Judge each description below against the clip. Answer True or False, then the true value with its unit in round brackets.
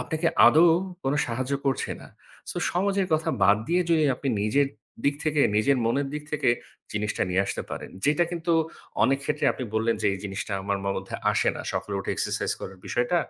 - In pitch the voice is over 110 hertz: True (135 Hz)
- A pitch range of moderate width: False (6.8 semitones)